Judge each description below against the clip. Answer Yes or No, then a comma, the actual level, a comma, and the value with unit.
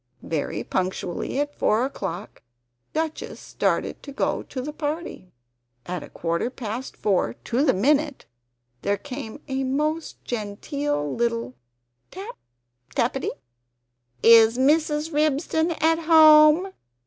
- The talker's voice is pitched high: Yes, very high, 275 Hz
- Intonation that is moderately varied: No, wide, 5.7 semitones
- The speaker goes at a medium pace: No, slow, 115 wpm